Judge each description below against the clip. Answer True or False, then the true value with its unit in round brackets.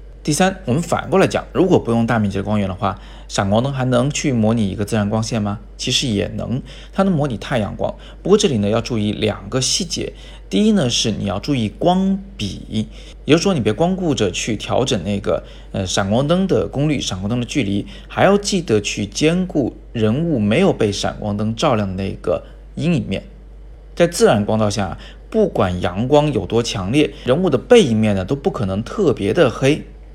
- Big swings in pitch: True (6.4 semitones)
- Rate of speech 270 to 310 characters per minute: True (290 characters per minute)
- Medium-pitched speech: False (110 Hz)